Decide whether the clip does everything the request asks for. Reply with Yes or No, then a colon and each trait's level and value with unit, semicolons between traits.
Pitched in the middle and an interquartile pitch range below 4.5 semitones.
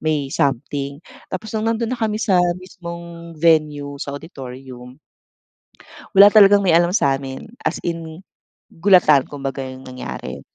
No: medium, 160 Hz; average, 5.1 semitones